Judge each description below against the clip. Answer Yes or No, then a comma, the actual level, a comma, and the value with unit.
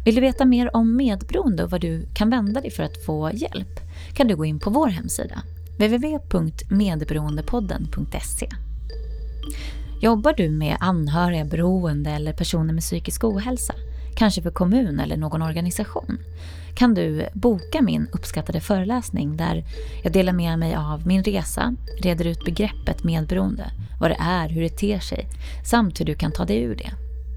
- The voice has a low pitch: No, medium, 165 Hz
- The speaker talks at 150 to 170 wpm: Yes, average, 160 wpm